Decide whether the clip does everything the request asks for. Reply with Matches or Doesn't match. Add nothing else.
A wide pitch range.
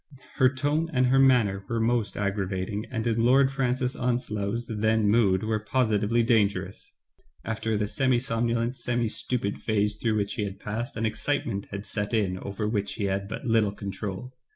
Doesn't match